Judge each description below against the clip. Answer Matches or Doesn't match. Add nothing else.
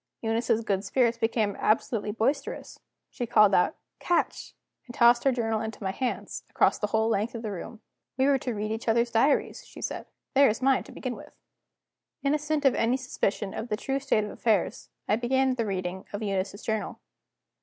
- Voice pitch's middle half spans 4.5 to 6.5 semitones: Doesn't match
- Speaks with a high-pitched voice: Matches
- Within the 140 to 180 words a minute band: Doesn't match